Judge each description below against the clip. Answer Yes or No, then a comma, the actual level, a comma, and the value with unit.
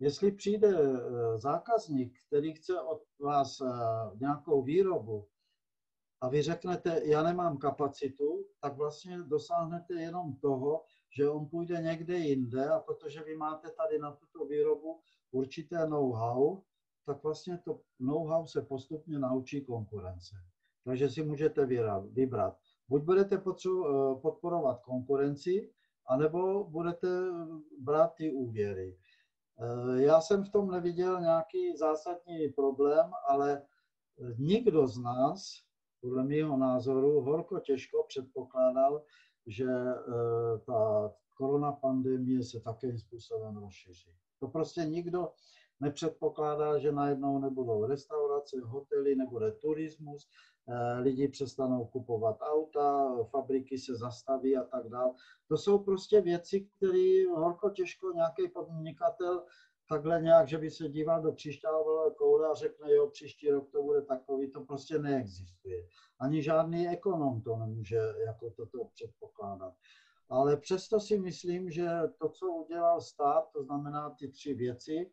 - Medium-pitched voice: Yes, medium, 150 Hz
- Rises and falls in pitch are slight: No, wide, 5.4 semitones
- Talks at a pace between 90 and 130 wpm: Yes, average, 125 wpm